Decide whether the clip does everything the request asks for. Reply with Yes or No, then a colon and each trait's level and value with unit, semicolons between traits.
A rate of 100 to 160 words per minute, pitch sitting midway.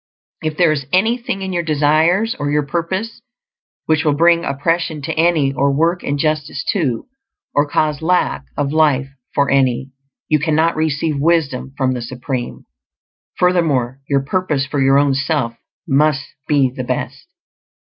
Yes: average, 150 wpm; medium, 150 Hz